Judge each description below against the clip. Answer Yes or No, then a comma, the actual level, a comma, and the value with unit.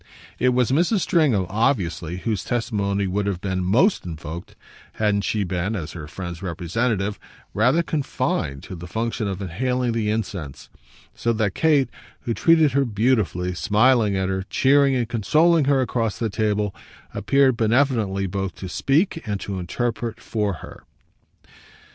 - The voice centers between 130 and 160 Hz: No, low, 110 Hz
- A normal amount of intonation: Yes, average, 5.0 semitones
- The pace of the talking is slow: No, average, 150 wpm